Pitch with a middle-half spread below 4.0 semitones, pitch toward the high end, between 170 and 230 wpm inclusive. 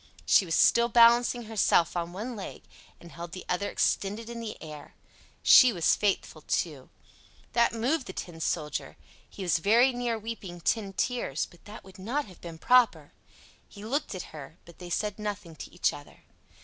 No: average, 5.2 semitones; high, 205 Hz; average, 180 wpm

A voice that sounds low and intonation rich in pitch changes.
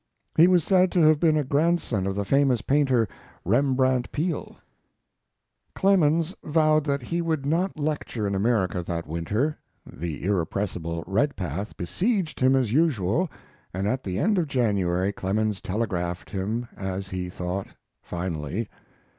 Yes: low, 120 Hz; wide, 8.3 semitones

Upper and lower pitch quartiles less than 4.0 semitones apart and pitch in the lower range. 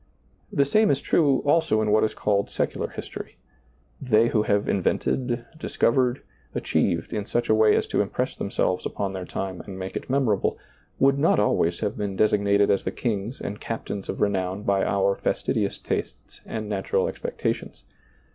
Yes: average, 3.5 semitones; low, 105 Hz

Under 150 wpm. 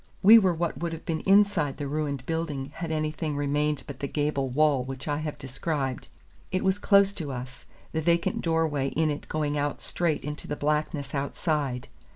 No: average, 195 wpm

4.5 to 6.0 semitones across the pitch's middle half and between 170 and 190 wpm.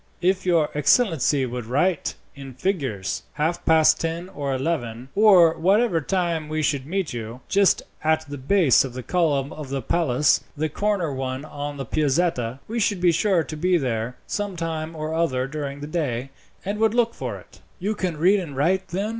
Yes: average, 5.0 semitones; average, 185 wpm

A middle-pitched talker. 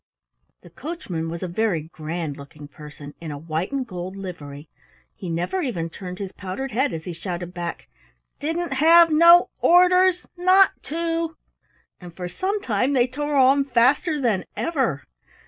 No: high, 210 Hz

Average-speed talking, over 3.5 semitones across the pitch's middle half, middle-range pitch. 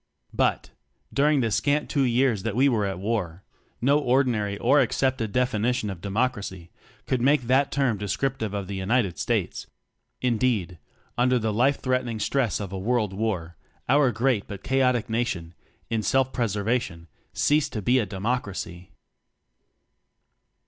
No: average, 150 wpm; average, 4.3 semitones; low, 115 Hz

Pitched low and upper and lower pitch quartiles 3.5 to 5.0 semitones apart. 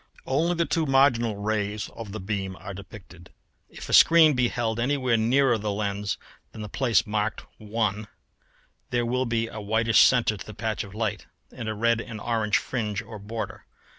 No: low, 110 Hz; narrow, 2.4 semitones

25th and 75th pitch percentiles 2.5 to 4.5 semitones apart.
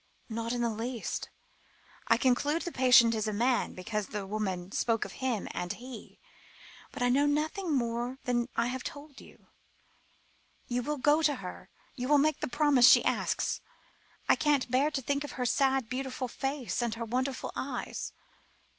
Yes: average, 3.4 semitones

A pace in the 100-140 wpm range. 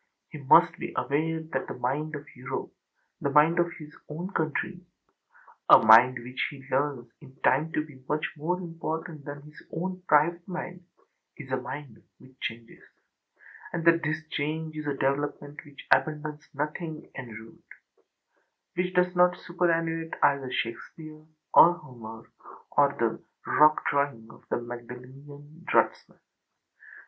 Yes: slow, 135 wpm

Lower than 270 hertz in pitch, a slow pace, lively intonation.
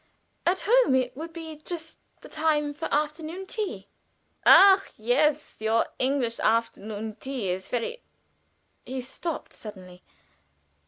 No: very high, 280 Hz; slow, 125 wpm; wide, 6.1 semitones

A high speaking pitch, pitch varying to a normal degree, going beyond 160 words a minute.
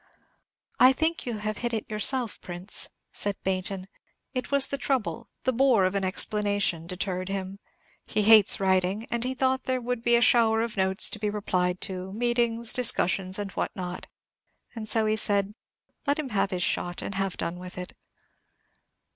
Yes: high, 210 Hz; average, 3.9 semitones; average, 180 wpm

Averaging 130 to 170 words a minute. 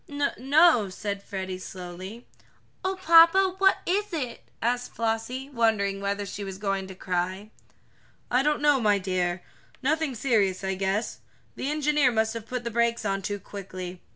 Yes: average, 160 wpm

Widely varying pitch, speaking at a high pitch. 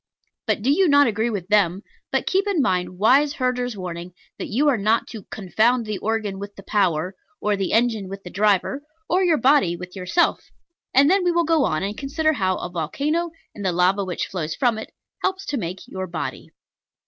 Yes: wide, 7.0 semitones; high, 215 Hz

